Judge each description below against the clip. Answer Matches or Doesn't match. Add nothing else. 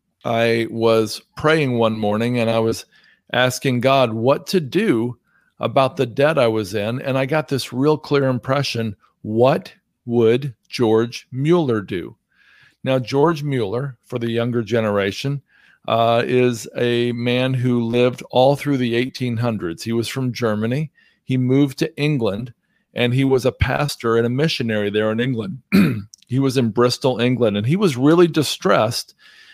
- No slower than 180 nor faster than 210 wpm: Doesn't match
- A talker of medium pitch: Doesn't match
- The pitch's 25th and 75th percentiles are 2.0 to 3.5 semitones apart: Matches